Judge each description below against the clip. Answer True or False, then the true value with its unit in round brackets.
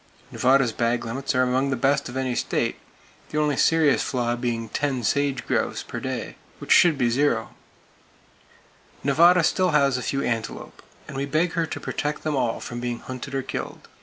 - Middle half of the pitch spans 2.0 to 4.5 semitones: True (3.0 semitones)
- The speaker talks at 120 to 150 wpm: False (185 wpm)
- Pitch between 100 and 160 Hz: True (135 Hz)